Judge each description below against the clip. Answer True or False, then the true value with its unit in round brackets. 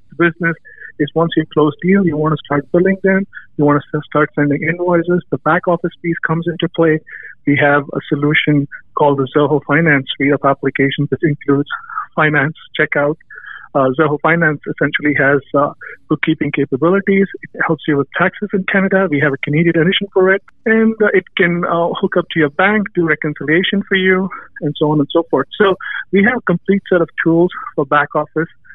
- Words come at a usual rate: True (195 wpm)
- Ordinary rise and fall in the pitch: True (3.5 semitones)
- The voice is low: False (160 Hz)